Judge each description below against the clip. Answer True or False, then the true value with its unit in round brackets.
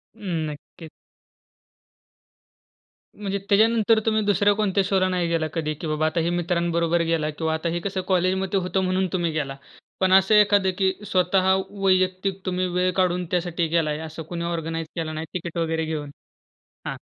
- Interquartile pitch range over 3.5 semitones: False (2.7 semitones)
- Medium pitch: True (180 Hz)